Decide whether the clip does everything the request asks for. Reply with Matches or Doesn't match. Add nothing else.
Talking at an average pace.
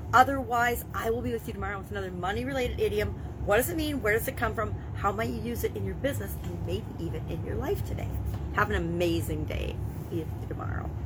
Doesn't match